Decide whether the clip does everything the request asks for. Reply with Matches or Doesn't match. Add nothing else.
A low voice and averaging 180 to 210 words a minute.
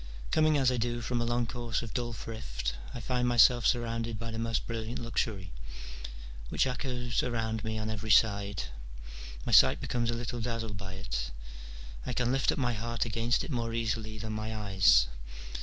Matches